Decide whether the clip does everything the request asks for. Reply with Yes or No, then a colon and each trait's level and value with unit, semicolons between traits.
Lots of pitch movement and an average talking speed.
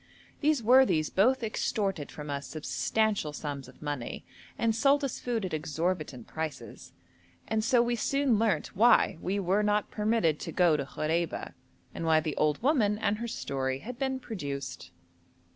Yes: wide, 7.3 semitones; average, 160 wpm